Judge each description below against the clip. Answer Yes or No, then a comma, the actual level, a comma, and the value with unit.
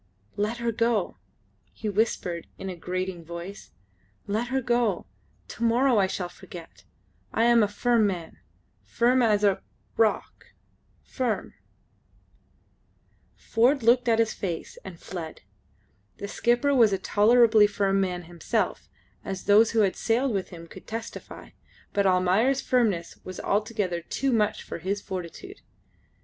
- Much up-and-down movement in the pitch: No, average, 4.1 semitones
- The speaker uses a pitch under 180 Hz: No, high, 210 Hz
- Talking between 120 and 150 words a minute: Yes, average, 140 wpm